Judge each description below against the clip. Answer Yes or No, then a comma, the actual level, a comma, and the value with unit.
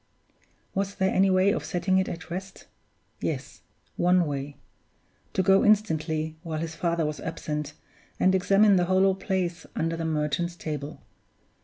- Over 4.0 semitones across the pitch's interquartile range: No, average, 3.1 semitones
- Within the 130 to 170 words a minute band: Yes, average, 150 wpm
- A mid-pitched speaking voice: Yes, medium, 175 Hz